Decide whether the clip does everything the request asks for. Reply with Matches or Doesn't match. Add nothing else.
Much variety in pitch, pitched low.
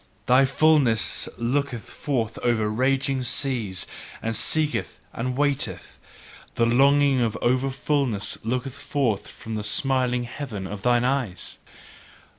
Doesn't match